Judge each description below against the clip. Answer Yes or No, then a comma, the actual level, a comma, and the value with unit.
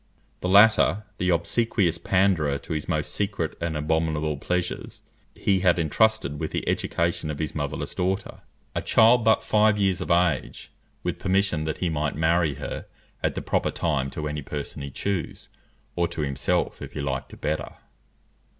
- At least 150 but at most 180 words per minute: Yes, average, 170 wpm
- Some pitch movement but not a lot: Yes, average, 4.1 semitones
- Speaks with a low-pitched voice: Yes, very low, 85 Hz